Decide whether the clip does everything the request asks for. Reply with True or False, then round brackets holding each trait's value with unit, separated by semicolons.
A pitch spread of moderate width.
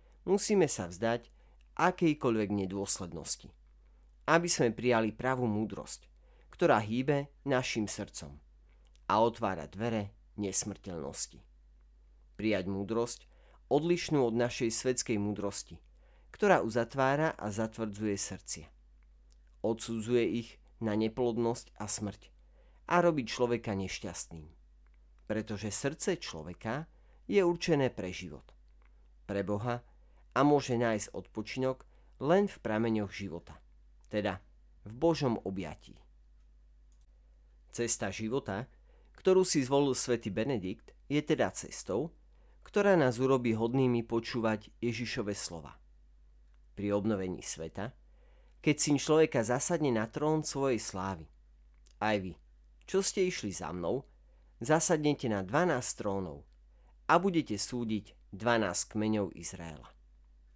False (7.5 semitones)